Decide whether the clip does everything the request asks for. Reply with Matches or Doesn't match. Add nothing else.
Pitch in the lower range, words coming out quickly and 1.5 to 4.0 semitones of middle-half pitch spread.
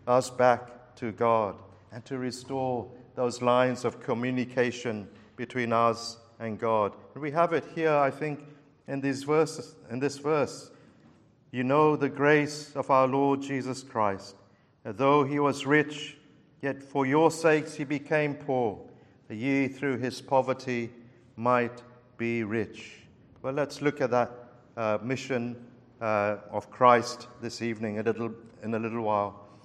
Doesn't match